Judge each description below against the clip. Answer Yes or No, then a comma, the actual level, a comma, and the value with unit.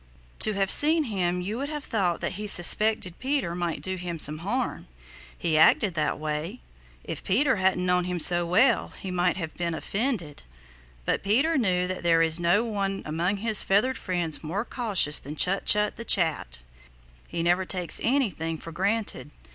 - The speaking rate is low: No, average, 180 wpm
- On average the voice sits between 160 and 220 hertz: Yes, medium, 185 Hz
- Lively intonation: No, average, 4.1 semitones